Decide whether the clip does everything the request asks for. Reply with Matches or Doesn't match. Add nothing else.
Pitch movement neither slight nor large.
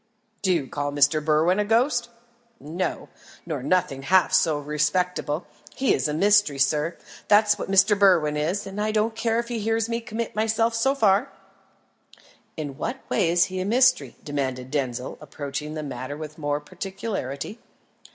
Doesn't match